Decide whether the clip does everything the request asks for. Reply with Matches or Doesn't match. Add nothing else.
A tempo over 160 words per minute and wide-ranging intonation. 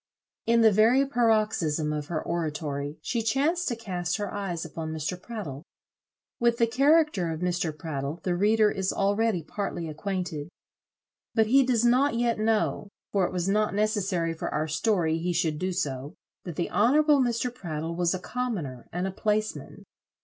Matches